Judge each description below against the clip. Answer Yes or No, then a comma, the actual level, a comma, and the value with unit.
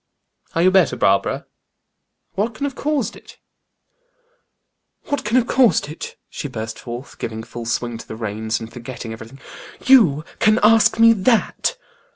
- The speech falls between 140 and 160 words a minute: Yes, average, 155 wpm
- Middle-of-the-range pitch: Yes, medium, 155 Hz